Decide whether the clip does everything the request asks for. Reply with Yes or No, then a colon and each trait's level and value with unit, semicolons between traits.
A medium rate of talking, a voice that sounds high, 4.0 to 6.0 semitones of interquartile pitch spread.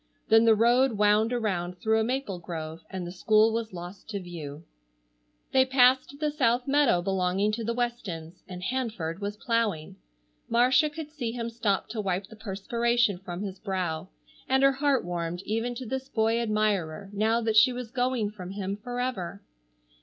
Yes: average, 175 wpm; high, 220 Hz; average, 4.5 semitones